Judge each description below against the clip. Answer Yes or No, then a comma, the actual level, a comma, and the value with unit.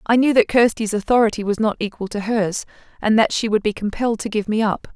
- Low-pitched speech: No, high, 215 Hz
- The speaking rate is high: Yes, fast, 240 wpm